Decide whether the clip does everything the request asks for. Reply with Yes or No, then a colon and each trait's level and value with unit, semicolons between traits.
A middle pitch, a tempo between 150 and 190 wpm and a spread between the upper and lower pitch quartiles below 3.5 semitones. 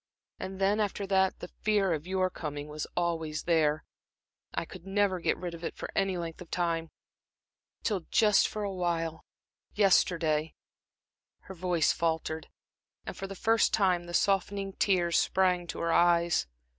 Yes: medium, 175 Hz; average, 160 wpm; average, 2.8 semitones